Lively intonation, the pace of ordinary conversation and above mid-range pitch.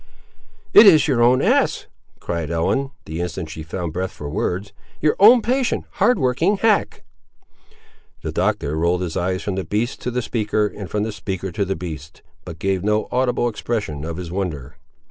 No: wide, 6.6 semitones; average, 185 wpm; very low, 95 Hz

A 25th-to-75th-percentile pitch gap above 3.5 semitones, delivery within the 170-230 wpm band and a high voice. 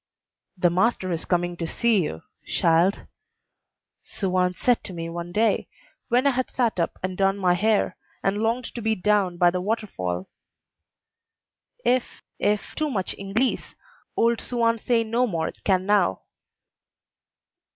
No: average, 4.5 semitones; average, 150 wpm; high, 195 Hz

